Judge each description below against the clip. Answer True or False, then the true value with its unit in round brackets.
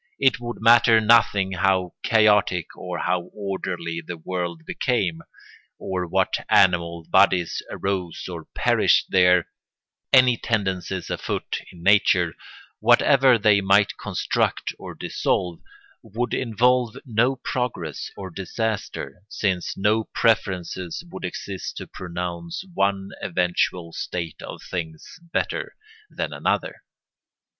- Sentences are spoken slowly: True (115 wpm)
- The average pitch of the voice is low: True (95 Hz)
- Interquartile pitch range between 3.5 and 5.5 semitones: True (4.1 semitones)